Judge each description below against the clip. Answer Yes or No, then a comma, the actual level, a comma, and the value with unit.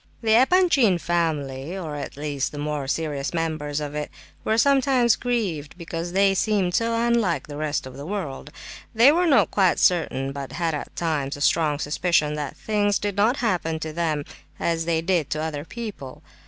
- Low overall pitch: No, medium, 165 Hz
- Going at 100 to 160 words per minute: No, average, 180 wpm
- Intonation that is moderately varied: No, wide, 5.9 semitones